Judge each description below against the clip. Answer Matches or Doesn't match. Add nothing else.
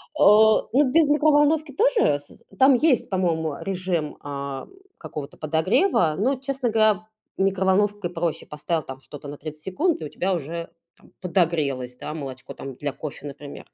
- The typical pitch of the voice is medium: Matches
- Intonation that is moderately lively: Doesn't match